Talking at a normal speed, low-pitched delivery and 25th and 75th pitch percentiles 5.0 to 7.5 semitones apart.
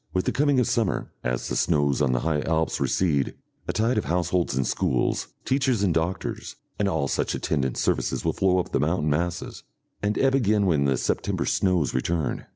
Yes: average, 195 wpm; very low, 85 Hz; wide, 5.5 semitones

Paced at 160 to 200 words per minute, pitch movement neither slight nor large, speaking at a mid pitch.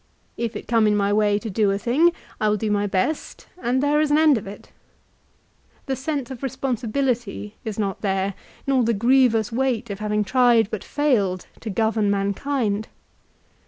No: average, 180 wpm; average, 4.2 semitones; high, 225 Hz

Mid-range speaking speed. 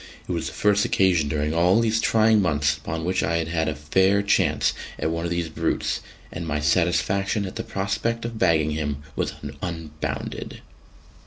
Yes: average, 180 wpm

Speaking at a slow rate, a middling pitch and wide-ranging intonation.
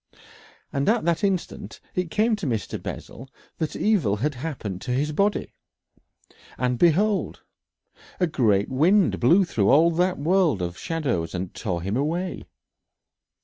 No: average, 145 wpm; medium, 150 Hz; wide, 7.5 semitones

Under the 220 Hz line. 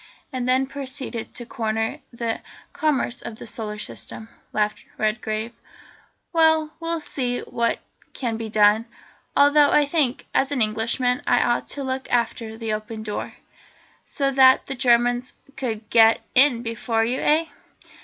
No: high, 240 Hz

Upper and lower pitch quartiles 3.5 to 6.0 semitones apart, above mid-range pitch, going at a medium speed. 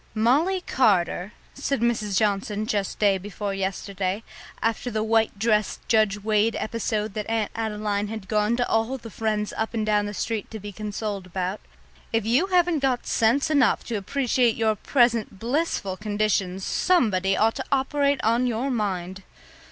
No: narrow, 2.6 semitones; high, 215 Hz; average, 160 wpm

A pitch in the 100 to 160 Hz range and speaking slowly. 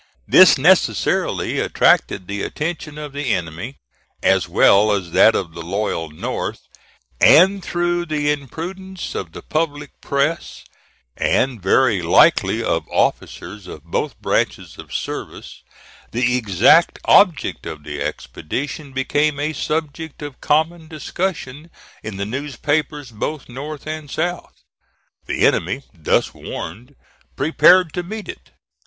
Yes: medium, 140 Hz; slow, 125 wpm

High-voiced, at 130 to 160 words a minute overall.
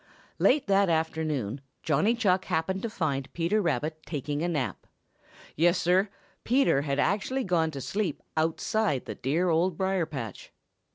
No: medium, 165 Hz; average, 150 wpm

